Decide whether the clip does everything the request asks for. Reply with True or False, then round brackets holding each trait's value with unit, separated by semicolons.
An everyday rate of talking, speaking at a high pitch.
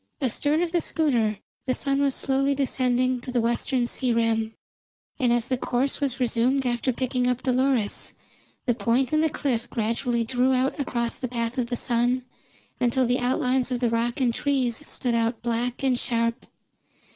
True (180 wpm; 250 Hz)